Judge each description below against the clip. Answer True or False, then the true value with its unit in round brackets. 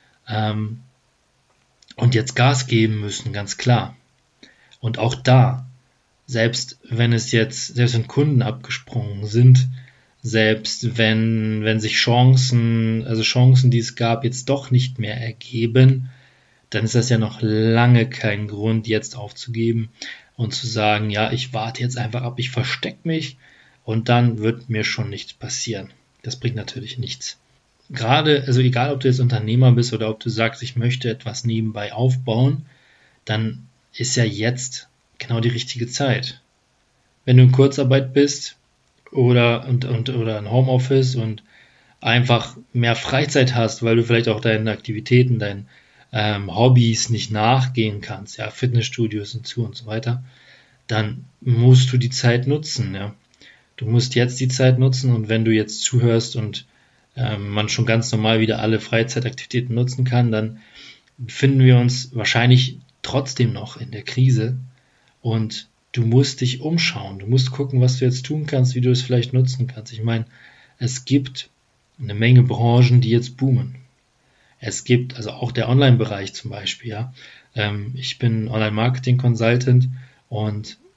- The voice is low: True (120 Hz)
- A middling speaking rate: True (155 wpm)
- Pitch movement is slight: True (2.3 semitones)